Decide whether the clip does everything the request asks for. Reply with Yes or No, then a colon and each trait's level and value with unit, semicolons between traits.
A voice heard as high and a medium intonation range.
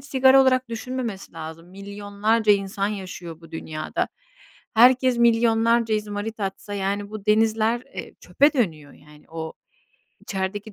Yes: high, 210 Hz; average, 3.3 semitones